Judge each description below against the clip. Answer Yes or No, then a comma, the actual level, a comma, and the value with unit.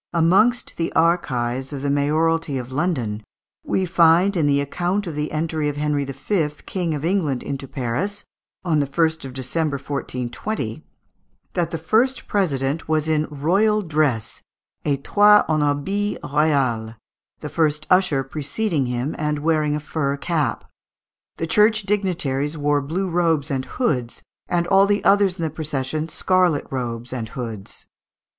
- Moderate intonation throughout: Yes, average, 4.1 semitones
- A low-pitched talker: No, medium, 155 Hz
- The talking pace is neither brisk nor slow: Yes, average, 150 wpm